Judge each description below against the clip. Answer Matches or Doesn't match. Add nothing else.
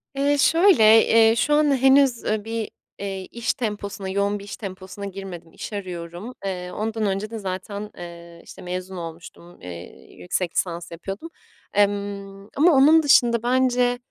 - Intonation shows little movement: Doesn't match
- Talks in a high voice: Matches